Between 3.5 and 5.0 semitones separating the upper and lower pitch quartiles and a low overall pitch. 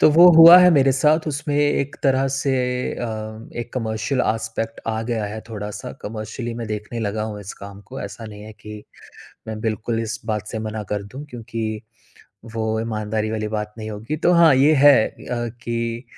Yes: average, 3.8 semitones; low, 115 Hz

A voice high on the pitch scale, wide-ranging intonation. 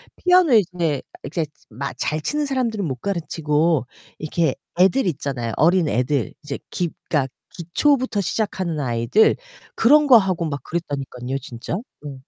No: medium, 165 Hz; wide, 6.3 semitones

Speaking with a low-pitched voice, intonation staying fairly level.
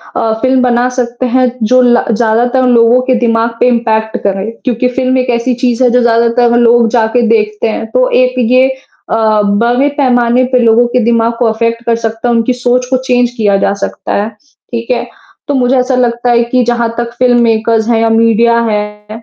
No: high, 235 Hz; narrow, 1.7 semitones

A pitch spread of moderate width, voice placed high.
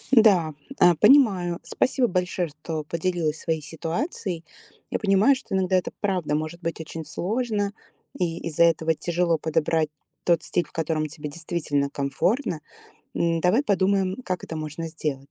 No: average, 3.2 semitones; medium, 170 Hz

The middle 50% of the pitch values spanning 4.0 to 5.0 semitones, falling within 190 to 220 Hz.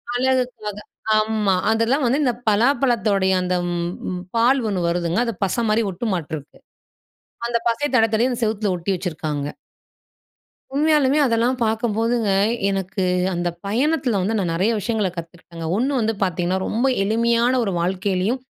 Yes: average, 4.4 semitones; high, 215 Hz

